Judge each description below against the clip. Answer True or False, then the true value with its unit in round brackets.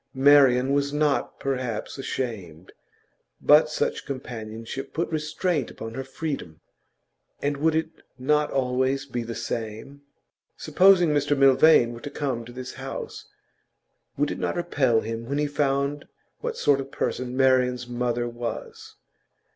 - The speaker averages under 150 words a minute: True (140 wpm)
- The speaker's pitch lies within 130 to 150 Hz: True (135 Hz)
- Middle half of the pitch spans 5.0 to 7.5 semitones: False (3.4 semitones)